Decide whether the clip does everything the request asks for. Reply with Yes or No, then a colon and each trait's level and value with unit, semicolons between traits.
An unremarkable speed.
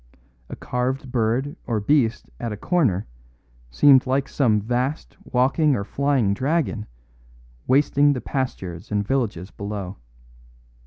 No: slow, 120 wpm